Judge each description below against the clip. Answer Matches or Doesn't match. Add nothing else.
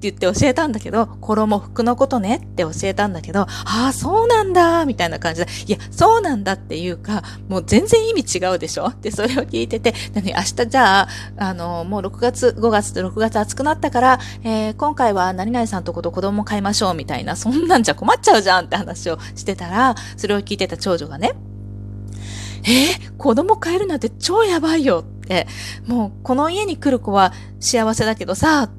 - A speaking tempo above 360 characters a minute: Matches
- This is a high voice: Matches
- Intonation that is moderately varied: Doesn't match